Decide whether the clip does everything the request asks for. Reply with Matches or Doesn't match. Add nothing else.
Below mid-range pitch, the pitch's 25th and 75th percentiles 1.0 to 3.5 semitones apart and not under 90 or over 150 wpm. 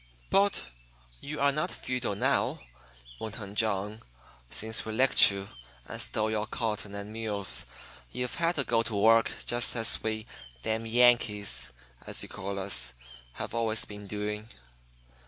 Matches